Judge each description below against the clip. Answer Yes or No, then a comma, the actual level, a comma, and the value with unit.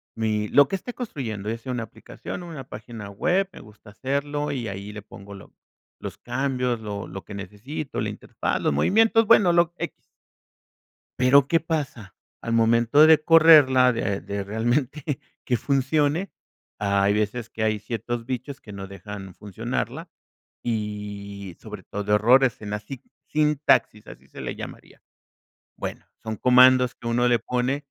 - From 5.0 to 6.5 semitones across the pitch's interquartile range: Yes, average, 5.3 semitones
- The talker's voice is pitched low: Yes, low, 120 Hz